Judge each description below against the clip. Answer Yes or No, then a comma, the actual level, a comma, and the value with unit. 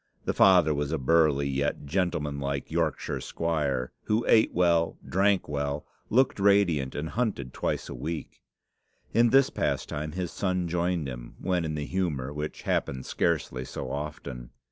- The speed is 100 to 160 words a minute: Yes, average, 150 wpm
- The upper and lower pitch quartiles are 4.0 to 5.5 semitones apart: Yes, average, 4.4 semitones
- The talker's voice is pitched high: No, very low, 80 Hz